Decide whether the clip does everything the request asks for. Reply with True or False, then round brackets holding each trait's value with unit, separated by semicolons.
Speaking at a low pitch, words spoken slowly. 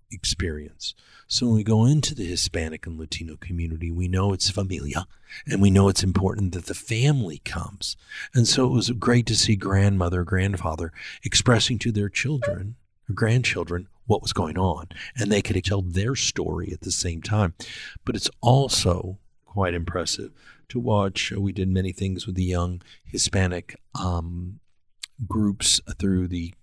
False (95 Hz; 160 wpm)